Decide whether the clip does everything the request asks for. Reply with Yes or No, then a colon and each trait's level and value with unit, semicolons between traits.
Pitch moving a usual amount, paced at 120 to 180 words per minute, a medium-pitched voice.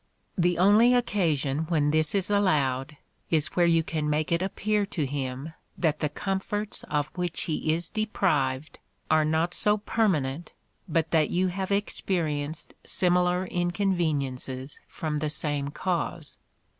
Yes: average, 3.9 semitones; average, 140 wpm; medium, 165 Hz